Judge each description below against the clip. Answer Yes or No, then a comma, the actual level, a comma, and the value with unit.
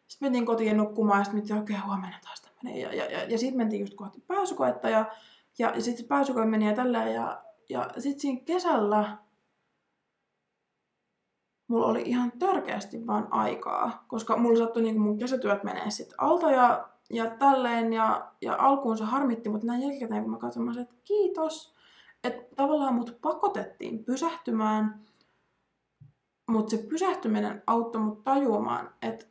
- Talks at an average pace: No, fast, 160 wpm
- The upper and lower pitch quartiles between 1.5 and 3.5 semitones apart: No, average, 4.2 semitones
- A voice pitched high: Yes, high, 230 Hz